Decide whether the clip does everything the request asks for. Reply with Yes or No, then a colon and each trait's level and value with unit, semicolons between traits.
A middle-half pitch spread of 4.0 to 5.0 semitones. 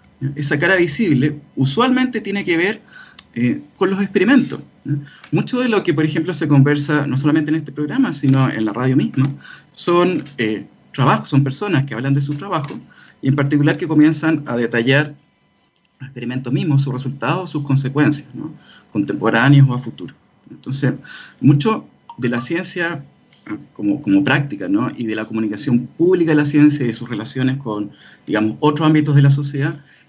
No: average, 3.6 semitones